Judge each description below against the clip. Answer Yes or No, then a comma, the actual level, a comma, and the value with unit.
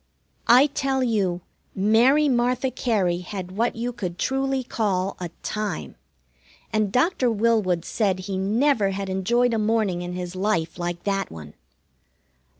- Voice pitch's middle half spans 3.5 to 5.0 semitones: Yes, average, 4.7 semitones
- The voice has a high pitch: Yes, high, 210 Hz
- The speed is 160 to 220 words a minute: No, average, 145 wpm